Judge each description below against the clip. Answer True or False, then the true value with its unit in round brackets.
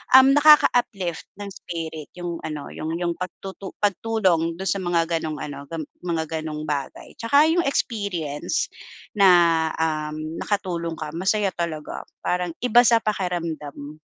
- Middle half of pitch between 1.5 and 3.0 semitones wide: False (4.4 semitones)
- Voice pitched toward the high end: False (175 Hz)